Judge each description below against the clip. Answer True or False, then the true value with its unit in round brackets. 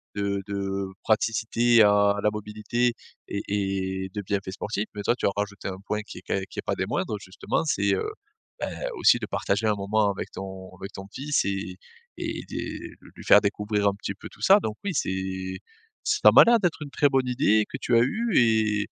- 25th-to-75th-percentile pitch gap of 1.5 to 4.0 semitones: True (3.1 semitones)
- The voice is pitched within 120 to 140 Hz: False (105 Hz)